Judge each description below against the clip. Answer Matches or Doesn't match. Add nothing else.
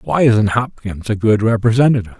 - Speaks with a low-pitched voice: Matches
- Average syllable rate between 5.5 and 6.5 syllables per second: Matches